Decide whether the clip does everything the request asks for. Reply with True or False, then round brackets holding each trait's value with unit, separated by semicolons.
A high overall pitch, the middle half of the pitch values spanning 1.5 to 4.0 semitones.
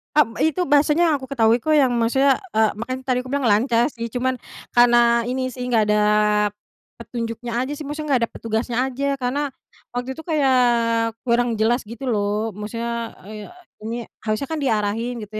True (245 Hz; 3.0 semitones)